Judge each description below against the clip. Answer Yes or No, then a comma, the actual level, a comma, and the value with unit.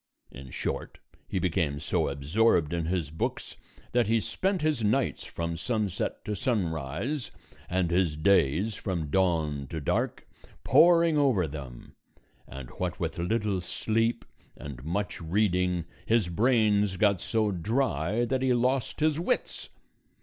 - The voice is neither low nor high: No, very low, 95 Hz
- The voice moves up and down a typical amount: No, wide, 6.2 semitones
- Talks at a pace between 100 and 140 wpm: Yes, slow, 135 wpm